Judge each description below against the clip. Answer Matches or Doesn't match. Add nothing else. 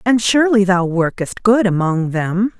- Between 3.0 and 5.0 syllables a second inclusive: Matches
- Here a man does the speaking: Doesn't match